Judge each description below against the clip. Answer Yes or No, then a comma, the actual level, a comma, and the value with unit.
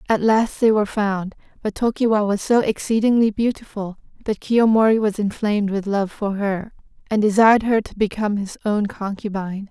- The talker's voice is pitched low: No, high, 210 Hz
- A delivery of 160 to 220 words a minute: Yes, average, 165 wpm